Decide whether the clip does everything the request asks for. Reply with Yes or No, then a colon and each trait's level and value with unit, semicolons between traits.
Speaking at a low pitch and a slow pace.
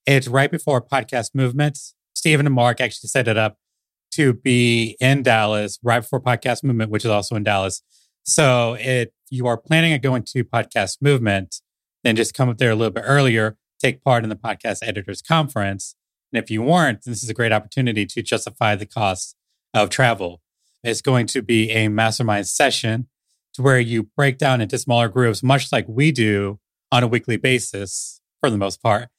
No: low, 120 Hz; average, 190 wpm